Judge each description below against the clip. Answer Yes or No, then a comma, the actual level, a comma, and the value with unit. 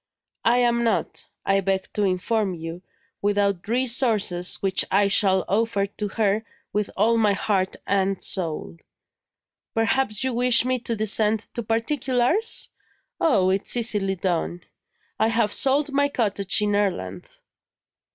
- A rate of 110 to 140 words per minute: Yes, slow, 135 wpm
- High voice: Yes, high, 210 Hz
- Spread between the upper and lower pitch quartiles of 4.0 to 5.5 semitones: No, average, 3.4 semitones